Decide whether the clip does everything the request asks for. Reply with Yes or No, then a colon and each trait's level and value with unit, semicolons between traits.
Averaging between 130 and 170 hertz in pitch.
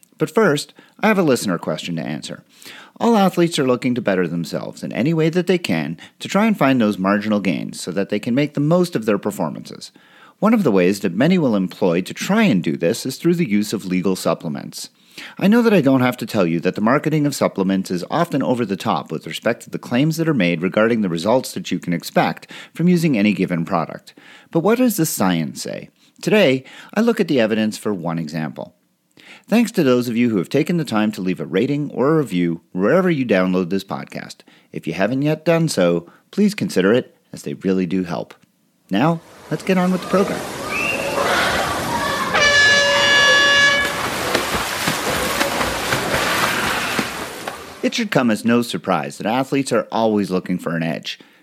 Yes: low, 135 Hz